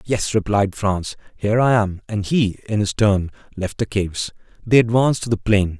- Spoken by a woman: No, male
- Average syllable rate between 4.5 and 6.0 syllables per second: Yes, 5.0 syllables/s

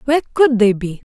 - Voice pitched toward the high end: Yes, high, 240 Hz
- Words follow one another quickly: Yes, fast, 215 wpm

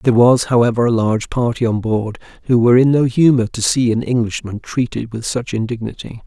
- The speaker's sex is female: No, male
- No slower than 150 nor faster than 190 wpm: No, average, 200 wpm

